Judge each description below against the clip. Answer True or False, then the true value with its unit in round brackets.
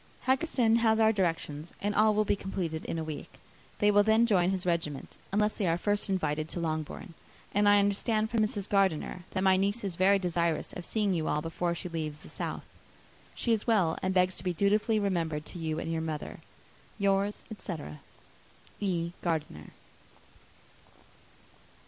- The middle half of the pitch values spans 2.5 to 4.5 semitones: True (4.0 semitones)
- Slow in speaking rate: False (175 wpm)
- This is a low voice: False (185 Hz)